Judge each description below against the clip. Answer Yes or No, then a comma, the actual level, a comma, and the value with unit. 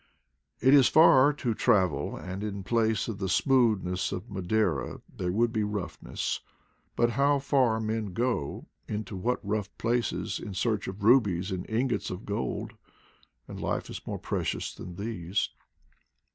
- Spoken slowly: No, average, 145 wpm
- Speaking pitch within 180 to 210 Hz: No, low, 105 Hz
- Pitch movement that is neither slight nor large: Yes, average, 3.9 semitones